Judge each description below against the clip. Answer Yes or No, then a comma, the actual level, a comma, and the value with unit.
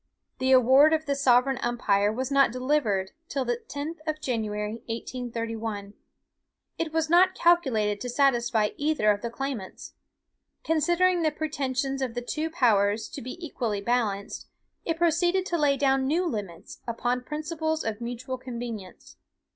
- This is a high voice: Yes, very high, 255 Hz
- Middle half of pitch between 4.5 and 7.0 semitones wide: Yes, average, 5.2 semitones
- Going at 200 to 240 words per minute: No, average, 145 wpm